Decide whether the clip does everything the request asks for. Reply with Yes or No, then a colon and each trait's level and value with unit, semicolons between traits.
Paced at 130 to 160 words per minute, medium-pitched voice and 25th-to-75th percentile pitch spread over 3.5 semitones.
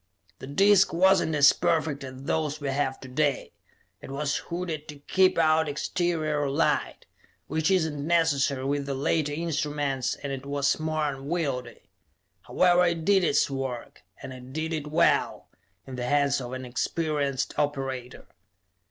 No: average, 155 wpm; medium, 145 Hz; average, 2.8 semitones